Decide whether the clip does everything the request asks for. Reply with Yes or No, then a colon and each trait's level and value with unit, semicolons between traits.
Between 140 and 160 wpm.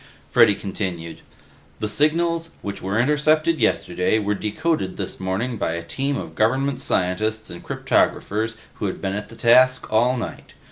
Yes: average, 155 wpm